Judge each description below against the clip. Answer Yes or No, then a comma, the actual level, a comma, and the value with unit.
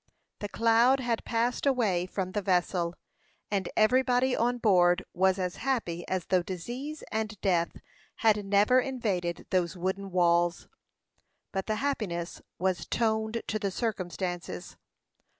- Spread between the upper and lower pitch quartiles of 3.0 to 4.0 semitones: No, average, 4.5 semitones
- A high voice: Yes, high, 200 Hz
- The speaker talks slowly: Yes, slow, 130 wpm